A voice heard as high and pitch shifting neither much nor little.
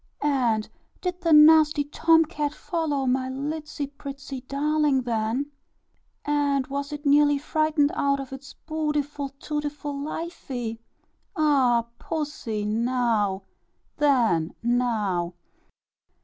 Yes: very high, 280 Hz; average, 3.3 semitones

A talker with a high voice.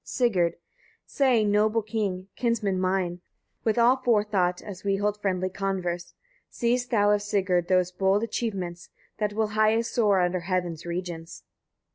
Yes: high, 200 Hz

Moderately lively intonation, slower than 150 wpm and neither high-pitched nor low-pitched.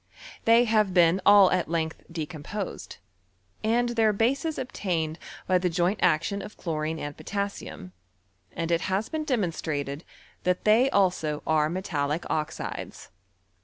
Yes: average, 5.0 semitones; slow, 135 wpm; medium, 180 Hz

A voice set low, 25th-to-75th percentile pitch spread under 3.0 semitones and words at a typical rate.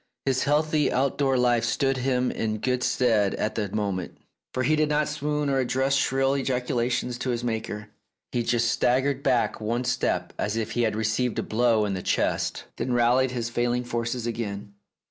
Yes: low, 125 Hz; narrow, 2.6 semitones; average, 185 wpm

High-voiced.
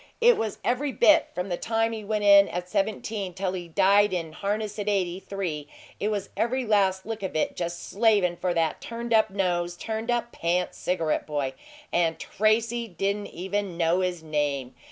Yes: high, 195 Hz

